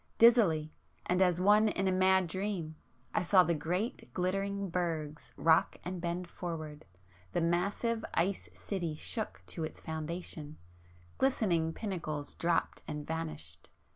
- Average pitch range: Yes, average, 3.3 semitones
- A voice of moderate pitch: Yes, medium, 175 Hz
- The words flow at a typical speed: No, slow, 130 wpm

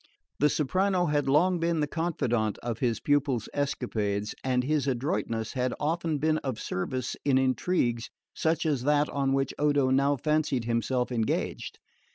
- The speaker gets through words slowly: No, average, 155 wpm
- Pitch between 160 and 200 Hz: No, medium, 140 Hz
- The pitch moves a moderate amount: Yes, average, 3.7 semitones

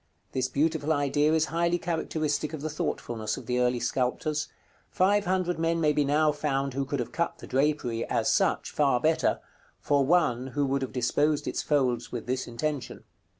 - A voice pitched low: No, medium, 145 Hz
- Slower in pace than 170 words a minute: No, average, 185 wpm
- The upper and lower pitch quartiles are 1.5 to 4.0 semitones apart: Yes, average, 3.5 semitones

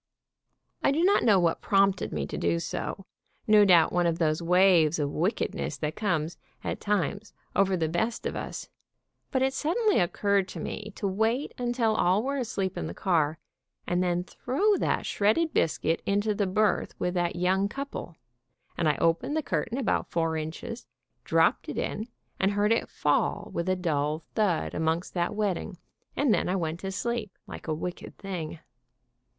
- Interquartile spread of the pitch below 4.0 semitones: No, average, 4.6 semitones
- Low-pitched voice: No, high, 190 Hz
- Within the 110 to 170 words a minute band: No, average, 180 wpm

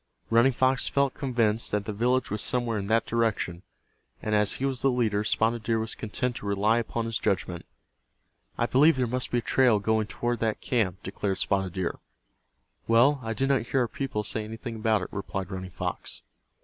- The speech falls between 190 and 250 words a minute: Yes, average, 200 wpm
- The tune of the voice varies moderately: Yes, average, 3.0 semitones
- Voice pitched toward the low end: Yes, low, 115 Hz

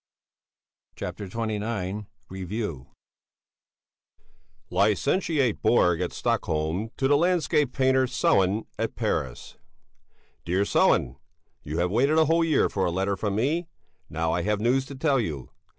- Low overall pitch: Yes, low, 105 Hz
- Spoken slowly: Yes, slow, 130 wpm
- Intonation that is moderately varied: No, wide, 6.7 semitones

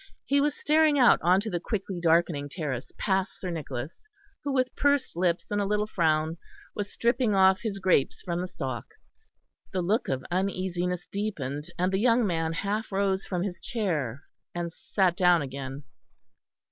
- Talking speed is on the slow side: No, average, 170 wpm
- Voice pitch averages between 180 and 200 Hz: Yes, medium, 185 Hz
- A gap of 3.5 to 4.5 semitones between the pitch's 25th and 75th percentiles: Yes, average, 4.1 semitones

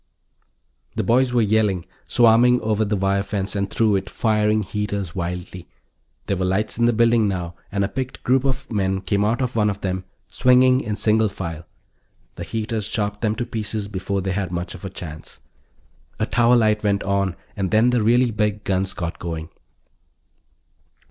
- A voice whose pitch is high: No, low, 105 Hz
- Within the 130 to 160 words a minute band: No, average, 180 wpm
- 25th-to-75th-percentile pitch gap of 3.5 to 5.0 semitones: No, average, 2.9 semitones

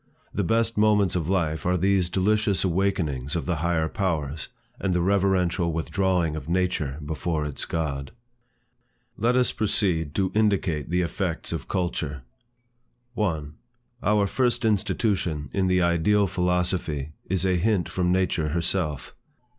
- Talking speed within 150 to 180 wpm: No, average, 140 wpm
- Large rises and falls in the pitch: No, average, 3.6 semitones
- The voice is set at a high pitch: No, very low, 90 Hz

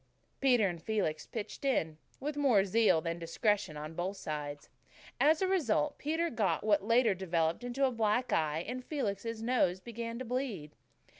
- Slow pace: No, average, 165 wpm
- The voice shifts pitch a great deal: Yes, wide, 6.8 semitones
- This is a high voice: Yes, high, 215 Hz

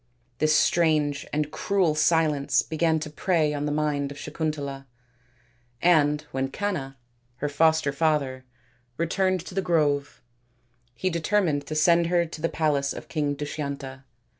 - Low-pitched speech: No, medium, 155 Hz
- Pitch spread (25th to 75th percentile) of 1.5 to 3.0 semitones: Yes, narrow, 2.6 semitones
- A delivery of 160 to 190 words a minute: No, average, 145 wpm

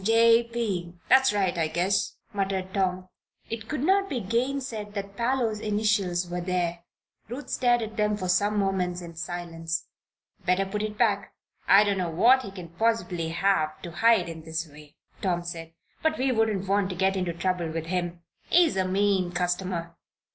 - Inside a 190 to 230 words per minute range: No, average, 175 wpm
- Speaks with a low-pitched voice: No, high, 195 Hz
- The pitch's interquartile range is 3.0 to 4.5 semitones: Yes, average, 4.0 semitones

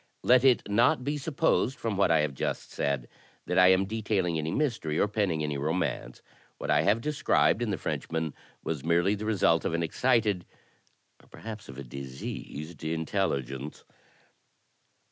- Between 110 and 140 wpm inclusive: No, average, 165 wpm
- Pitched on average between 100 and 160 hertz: No, very low, 90 Hz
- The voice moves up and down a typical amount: No, wide, 6.3 semitones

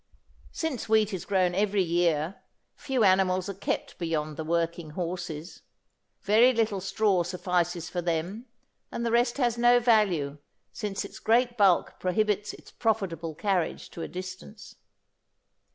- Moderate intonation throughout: Yes, average, 4.2 semitones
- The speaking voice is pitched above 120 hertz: Yes, high, 190 Hz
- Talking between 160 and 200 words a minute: No, average, 140 wpm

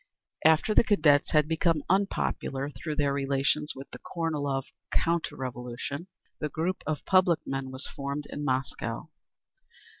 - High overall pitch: No, medium, 145 Hz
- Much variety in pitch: No, average, 3.1 semitones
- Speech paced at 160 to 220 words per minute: No, average, 145 wpm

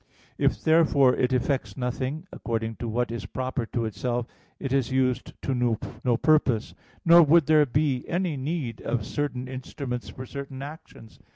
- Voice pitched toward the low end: Yes, low, 130 Hz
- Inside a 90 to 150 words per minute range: No, average, 160 wpm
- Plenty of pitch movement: No, average, 3.2 semitones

